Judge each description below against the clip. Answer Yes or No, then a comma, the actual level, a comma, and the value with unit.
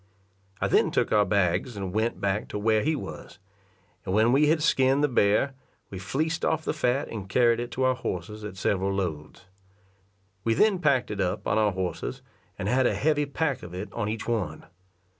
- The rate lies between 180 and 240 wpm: Yes, average, 200 wpm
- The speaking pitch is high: No, low, 110 Hz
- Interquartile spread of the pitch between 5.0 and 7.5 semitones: Yes, wide, 5.5 semitones